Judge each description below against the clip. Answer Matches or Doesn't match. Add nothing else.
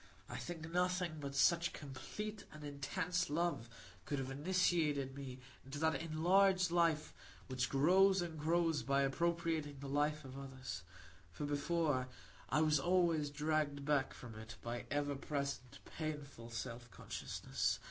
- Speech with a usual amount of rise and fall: Matches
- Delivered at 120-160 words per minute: Matches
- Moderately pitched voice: Matches